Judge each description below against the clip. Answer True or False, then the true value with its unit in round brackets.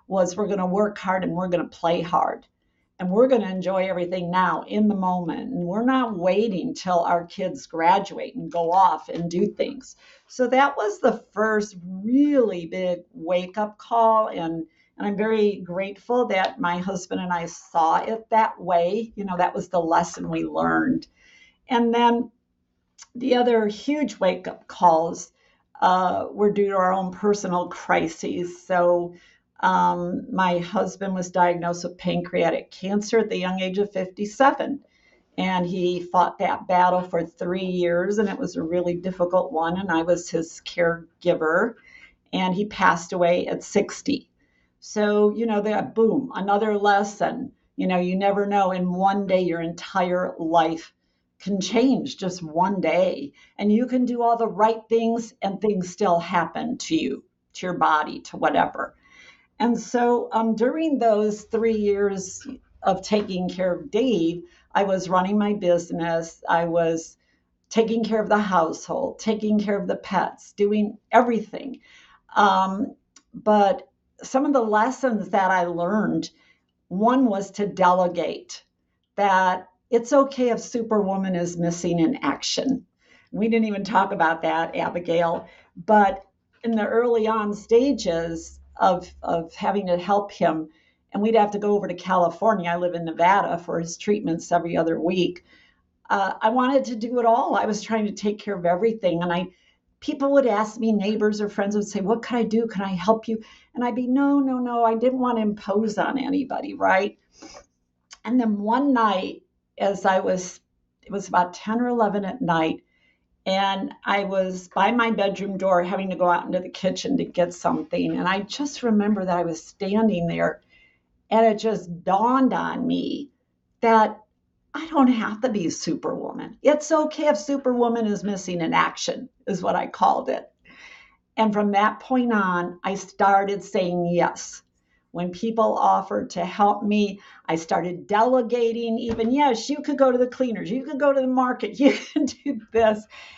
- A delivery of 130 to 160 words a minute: False (170 wpm)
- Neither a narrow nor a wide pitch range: True (4.2 semitones)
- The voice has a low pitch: False (205 Hz)